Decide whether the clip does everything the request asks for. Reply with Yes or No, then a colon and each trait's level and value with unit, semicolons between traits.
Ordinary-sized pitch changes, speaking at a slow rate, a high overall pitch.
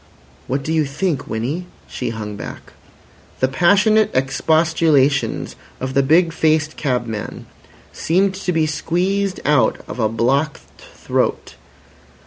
No: average, 4.6 semitones; slow, 120 wpm; medium, 155 Hz